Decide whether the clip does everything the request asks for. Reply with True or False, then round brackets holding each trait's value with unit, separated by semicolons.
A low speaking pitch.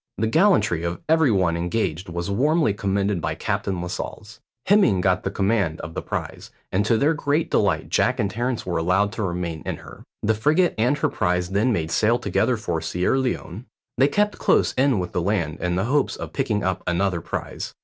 True (100 Hz)